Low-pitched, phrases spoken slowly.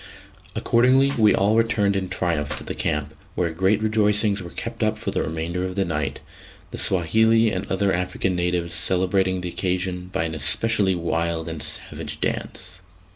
No: very low, 90 Hz; average, 170 wpm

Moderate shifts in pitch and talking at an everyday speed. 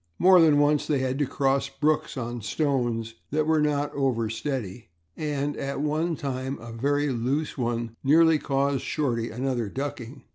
Yes: average, 3.5 semitones; average, 160 wpm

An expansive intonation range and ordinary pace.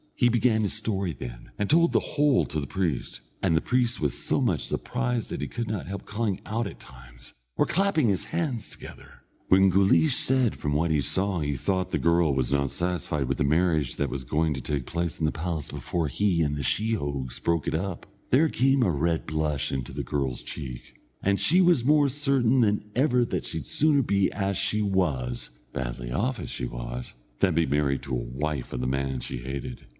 No: wide, 8.3 semitones; fast, 210 wpm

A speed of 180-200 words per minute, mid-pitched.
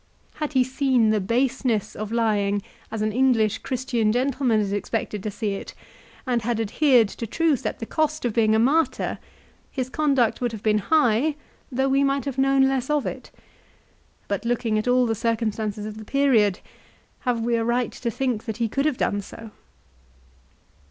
No: average, 185 wpm; high, 235 Hz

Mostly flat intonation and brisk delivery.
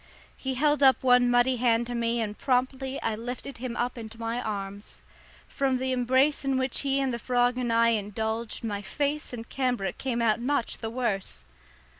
No: narrow, 2.3 semitones; average, 190 wpm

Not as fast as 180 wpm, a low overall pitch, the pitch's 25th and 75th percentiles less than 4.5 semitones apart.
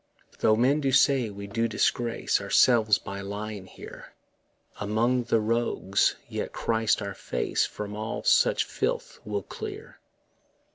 Yes: slow, 135 wpm; low, 110 Hz; narrow, 2.5 semitones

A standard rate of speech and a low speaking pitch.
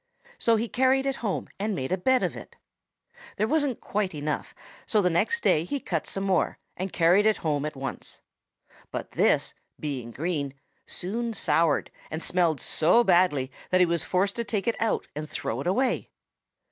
No: average, 185 wpm; medium, 185 Hz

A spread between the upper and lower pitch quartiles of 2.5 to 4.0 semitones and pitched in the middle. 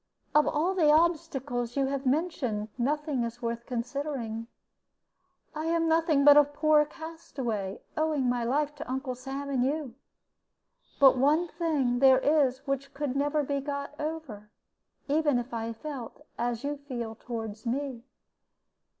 No: average, 3.7 semitones; very high, 275 Hz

